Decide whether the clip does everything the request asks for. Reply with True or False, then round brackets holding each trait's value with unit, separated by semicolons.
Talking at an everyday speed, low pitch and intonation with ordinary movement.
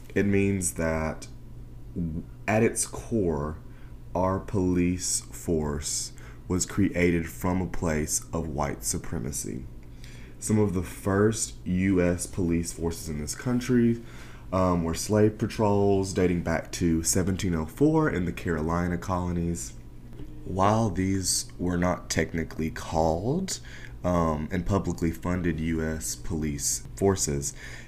False (110 wpm; 90 Hz; 3.7 semitones)